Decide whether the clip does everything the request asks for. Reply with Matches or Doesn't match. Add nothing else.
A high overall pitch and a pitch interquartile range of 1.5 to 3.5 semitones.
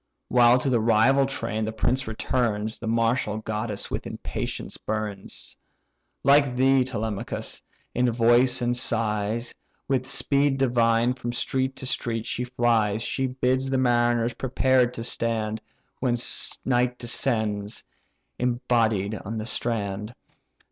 Doesn't match